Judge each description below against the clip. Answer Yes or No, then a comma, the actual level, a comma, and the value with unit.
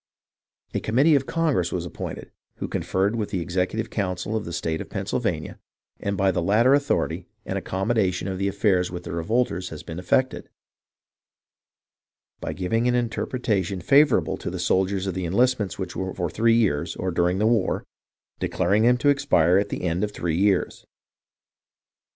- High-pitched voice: No, very low, 95 Hz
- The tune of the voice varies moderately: Yes, average, 4.2 semitones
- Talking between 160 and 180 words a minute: Yes, average, 170 wpm